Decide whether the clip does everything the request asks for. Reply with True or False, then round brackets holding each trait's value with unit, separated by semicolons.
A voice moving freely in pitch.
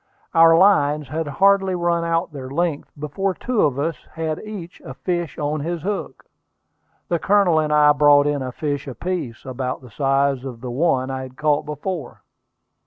False (3.9 semitones)